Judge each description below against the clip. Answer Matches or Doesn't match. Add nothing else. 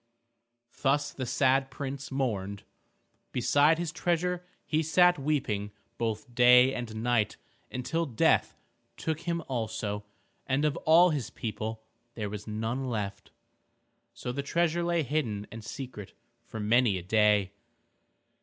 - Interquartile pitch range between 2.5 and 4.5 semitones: Doesn't match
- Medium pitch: Doesn't match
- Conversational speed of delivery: Doesn't match